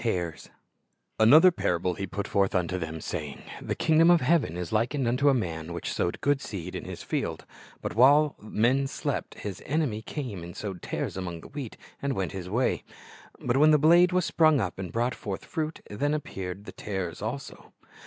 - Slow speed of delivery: No, average, 200 wpm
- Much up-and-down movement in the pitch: Yes, wide, 7.9 semitones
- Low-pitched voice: Yes, low, 110 Hz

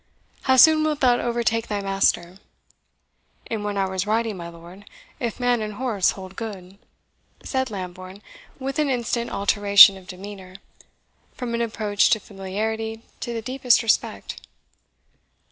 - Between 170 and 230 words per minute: No, average, 140 wpm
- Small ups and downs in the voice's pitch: No, average, 3.5 semitones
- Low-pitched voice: No, high, 215 Hz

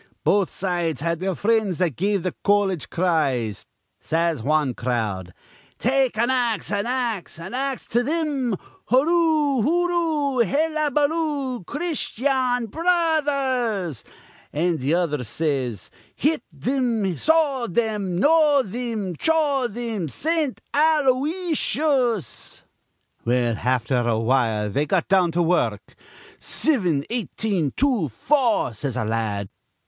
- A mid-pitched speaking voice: No, high, 220 Hz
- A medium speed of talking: No, slow, 120 wpm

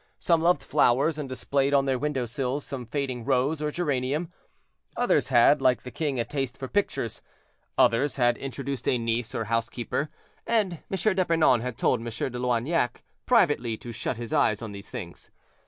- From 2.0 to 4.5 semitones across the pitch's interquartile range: Yes, average, 3.8 semitones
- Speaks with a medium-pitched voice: No, low, 130 Hz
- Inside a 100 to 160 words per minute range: No, average, 175 wpm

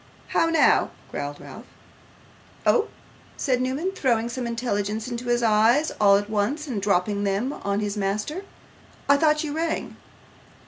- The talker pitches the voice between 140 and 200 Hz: No, high, 235 Hz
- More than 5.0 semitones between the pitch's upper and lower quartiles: Yes, wide, 5.6 semitones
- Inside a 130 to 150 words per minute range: Yes, average, 145 wpm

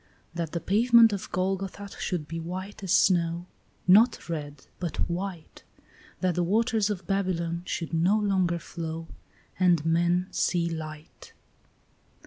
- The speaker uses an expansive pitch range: No, average, 2.8 semitones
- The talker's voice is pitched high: No, medium, 180 Hz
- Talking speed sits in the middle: No, slow, 130 wpm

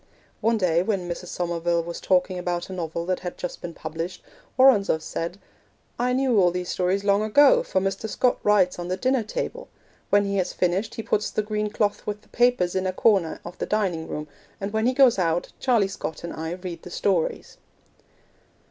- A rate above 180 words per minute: Yes, average, 200 wpm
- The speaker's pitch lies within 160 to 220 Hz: Yes, high, 190 Hz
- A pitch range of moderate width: Yes, average, 3.4 semitones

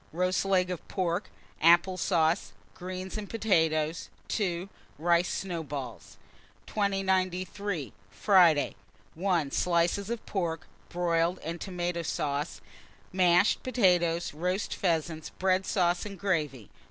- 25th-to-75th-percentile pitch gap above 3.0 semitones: No, narrow, 2.4 semitones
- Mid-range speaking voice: Yes, medium, 175 Hz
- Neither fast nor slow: No, slow, 105 wpm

